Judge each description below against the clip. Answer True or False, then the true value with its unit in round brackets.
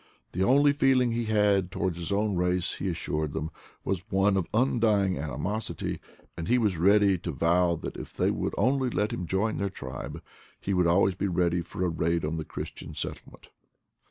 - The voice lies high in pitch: False (95 Hz)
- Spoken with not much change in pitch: False (3.7 semitones)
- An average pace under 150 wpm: False (195 wpm)